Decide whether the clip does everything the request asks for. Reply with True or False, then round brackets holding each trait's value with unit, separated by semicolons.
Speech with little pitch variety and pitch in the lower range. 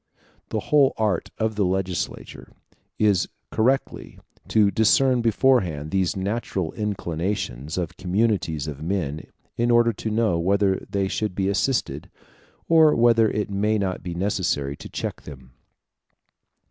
False (4.0 semitones; 100 Hz)